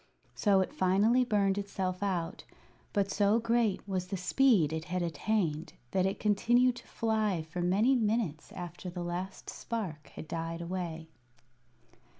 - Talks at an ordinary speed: Yes, average, 150 wpm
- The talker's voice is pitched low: No, high, 190 Hz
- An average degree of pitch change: Yes, average, 3.7 semitones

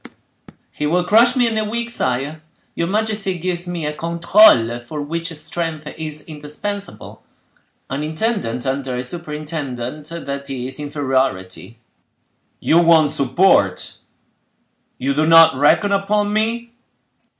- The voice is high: No, medium, 155 Hz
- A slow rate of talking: Yes, slow, 115 wpm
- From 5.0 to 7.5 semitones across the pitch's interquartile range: Yes, wide, 5.5 semitones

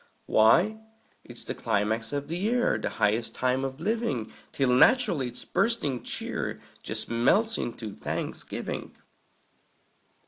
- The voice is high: No, low, 135 Hz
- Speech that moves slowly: Yes, slow, 125 wpm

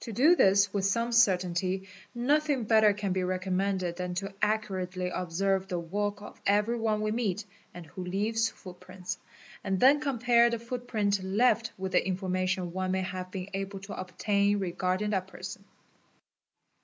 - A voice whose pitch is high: Yes, high, 195 Hz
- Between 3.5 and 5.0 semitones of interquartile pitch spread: No, average, 2.8 semitones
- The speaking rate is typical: Yes, average, 165 wpm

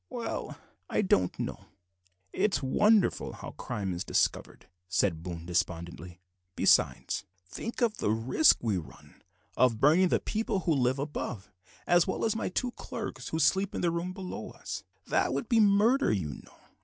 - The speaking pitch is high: No, medium, 155 Hz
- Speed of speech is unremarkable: Yes, average, 165 wpm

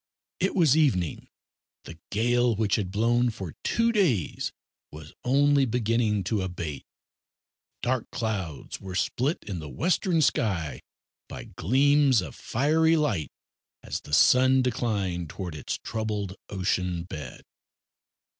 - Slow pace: Yes, slow, 125 wpm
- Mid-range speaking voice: No, low, 110 Hz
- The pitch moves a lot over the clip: Yes, wide, 6.3 semitones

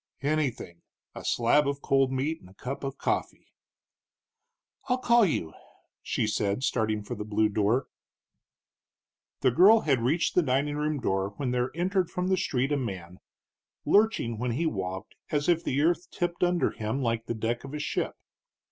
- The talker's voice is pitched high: No, low, 135 Hz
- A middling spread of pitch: No, wide, 6.4 semitones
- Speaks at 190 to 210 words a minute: No, average, 175 wpm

